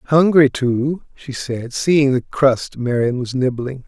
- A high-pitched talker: No, low, 135 Hz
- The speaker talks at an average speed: Yes, average, 155 wpm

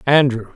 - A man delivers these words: Yes, male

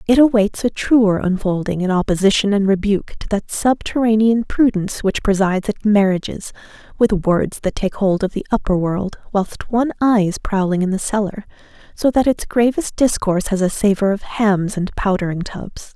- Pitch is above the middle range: Yes, high, 205 Hz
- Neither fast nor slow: Yes, average, 175 wpm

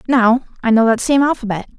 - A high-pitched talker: Yes, high, 240 Hz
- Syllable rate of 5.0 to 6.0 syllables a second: Yes, 5.9 syllables/s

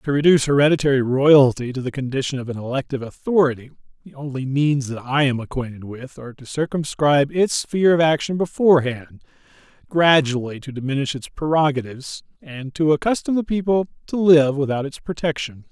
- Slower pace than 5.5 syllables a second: No, 5.8 syllables/s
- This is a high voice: No, medium, 140 Hz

